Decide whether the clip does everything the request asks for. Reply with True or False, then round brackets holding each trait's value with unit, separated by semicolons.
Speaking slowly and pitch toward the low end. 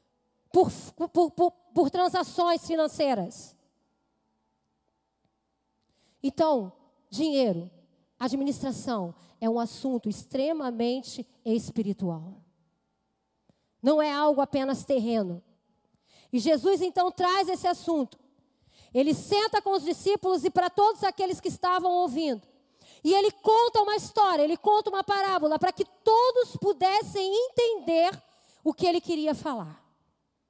False (110 wpm; 315 Hz)